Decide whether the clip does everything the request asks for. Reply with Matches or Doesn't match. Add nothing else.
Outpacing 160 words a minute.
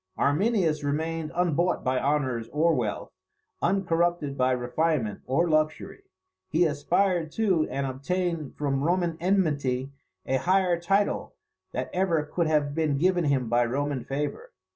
Doesn't match